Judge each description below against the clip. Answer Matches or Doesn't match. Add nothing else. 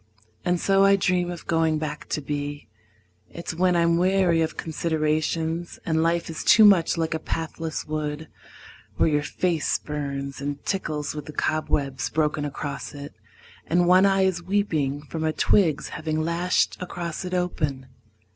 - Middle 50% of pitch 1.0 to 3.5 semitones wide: Matches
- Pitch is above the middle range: Doesn't match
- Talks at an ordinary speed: Matches